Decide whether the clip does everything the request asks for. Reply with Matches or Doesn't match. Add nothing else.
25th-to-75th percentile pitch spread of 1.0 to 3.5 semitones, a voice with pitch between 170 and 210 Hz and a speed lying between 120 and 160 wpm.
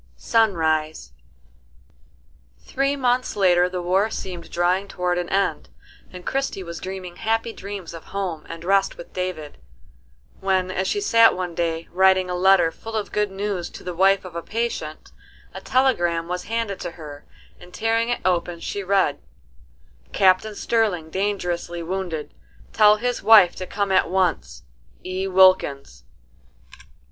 Matches